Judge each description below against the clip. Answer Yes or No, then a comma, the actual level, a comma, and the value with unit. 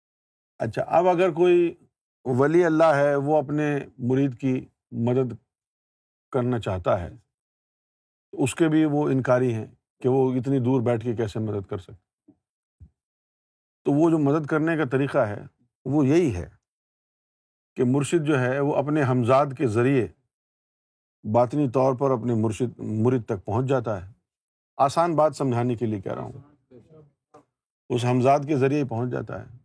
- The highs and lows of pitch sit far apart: No, average, 3.4 semitones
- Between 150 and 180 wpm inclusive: Yes, average, 160 wpm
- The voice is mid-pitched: No, low, 130 Hz